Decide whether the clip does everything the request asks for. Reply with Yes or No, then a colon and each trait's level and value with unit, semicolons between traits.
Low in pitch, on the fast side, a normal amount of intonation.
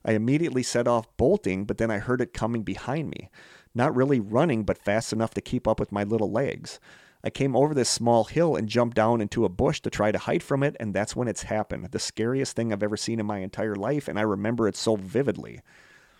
Yes: low, 115 Hz; fast, 240 wpm; average, 3.0 semitones